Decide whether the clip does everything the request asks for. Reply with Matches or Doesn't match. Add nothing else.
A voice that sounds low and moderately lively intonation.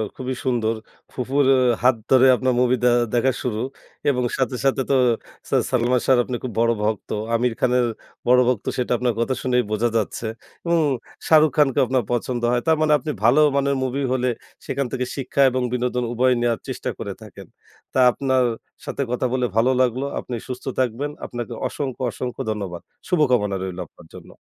Doesn't match